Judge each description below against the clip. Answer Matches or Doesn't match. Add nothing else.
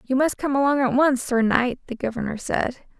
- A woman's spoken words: Matches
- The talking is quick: Matches